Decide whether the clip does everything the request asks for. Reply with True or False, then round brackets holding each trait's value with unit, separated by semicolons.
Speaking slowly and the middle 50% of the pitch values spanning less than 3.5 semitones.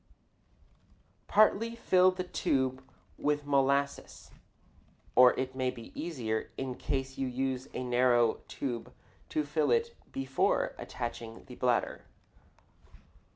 True (110 wpm; 2.8 semitones)